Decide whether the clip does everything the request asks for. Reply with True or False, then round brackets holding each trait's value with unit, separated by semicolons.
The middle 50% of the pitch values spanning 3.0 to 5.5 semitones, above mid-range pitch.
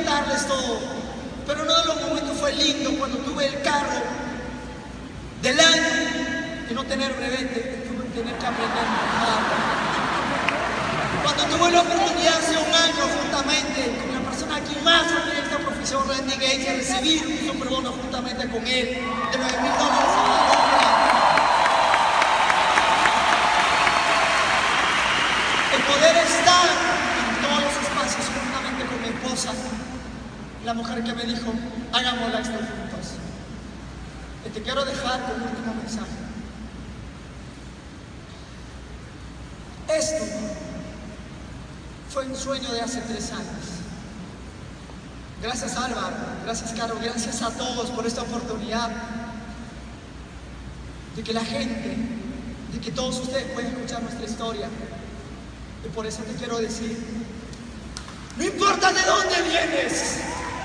True (3.7 semitones; 250 Hz)